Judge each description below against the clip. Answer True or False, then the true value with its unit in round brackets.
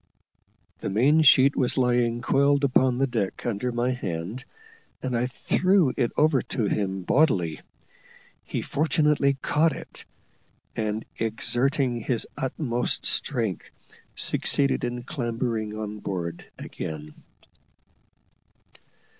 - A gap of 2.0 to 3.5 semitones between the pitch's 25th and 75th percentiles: False (4.2 semitones)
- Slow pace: True (110 wpm)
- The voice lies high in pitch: False (120 Hz)